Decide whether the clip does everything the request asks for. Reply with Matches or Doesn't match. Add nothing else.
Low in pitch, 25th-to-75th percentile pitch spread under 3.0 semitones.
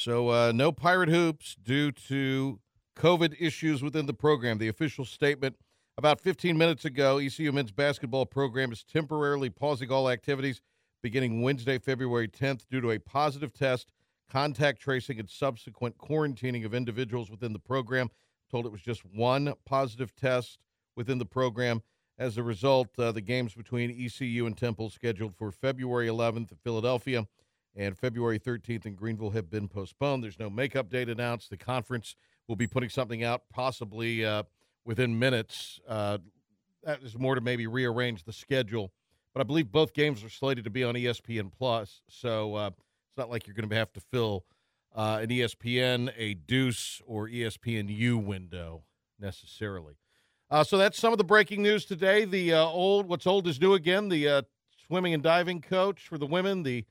Doesn't match